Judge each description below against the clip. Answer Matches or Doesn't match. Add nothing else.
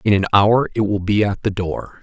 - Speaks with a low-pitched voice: Matches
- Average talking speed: Doesn't match